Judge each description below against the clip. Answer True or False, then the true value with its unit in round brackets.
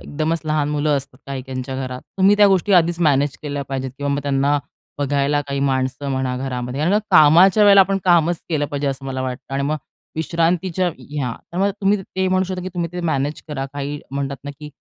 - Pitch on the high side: False (145 Hz)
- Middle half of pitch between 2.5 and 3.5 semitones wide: False (4.2 semitones)